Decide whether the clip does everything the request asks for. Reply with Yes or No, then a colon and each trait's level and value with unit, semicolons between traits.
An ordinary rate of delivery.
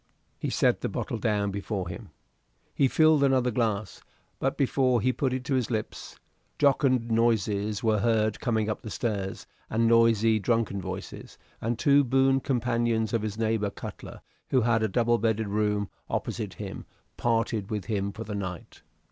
Yes: average, 165 wpm